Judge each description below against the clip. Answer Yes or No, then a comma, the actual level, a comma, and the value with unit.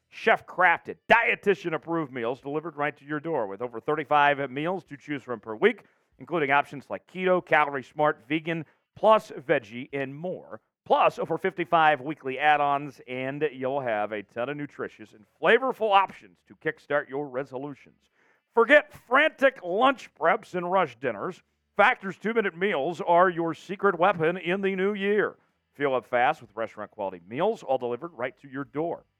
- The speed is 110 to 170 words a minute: Yes, average, 160 wpm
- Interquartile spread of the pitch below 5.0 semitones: No, wide, 5.4 semitones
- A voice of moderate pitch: Yes, medium, 150 Hz